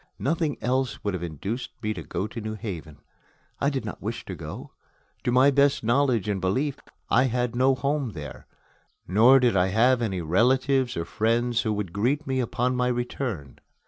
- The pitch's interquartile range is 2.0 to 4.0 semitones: No, average, 4.8 semitones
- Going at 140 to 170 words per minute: No, average, 185 wpm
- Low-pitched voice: Yes, low, 120 Hz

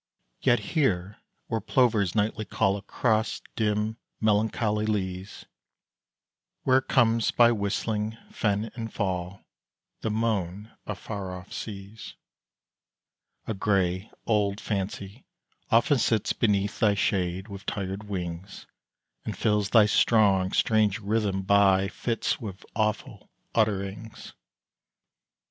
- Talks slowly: Yes, slow, 110 wpm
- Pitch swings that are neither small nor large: No, narrow, 2.3 semitones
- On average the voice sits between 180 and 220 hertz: No, low, 105 Hz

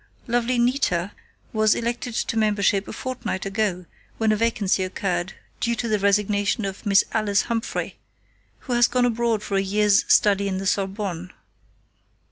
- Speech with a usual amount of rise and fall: Yes, average, 3.0 semitones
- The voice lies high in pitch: Yes, high, 210 Hz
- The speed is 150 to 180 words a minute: Yes, average, 155 wpm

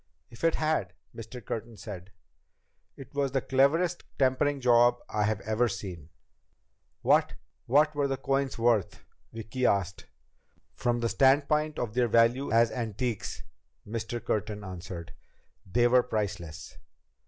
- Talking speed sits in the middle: No, slow, 130 wpm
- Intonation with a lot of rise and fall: No, average, 4.0 semitones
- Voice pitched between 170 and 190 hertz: No, low, 120 Hz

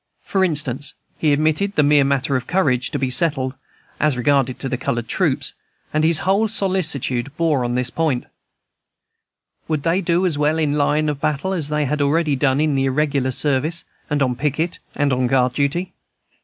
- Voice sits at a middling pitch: Yes, medium, 145 Hz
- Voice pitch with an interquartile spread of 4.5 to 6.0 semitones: No, average, 3.2 semitones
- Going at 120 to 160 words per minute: No, average, 180 wpm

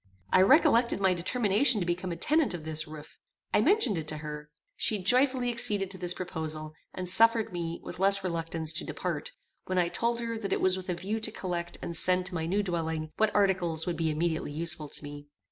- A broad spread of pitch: No, average, 4.5 semitones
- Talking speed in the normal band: No, fast, 215 wpm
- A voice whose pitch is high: No, medium, 180 Hz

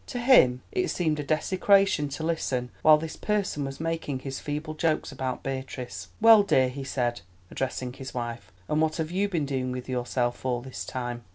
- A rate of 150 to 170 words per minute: No, average, 190 wpm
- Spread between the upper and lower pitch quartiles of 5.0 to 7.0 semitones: No, average, 4.2 semitones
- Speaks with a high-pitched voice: No, medium, 140 Hz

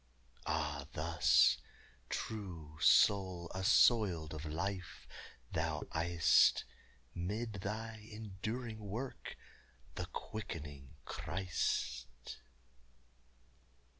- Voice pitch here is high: No, very low, 90 Hz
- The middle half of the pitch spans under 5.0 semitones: No, wide, 5.4 semitones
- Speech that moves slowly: Yes, slow, 70 wpm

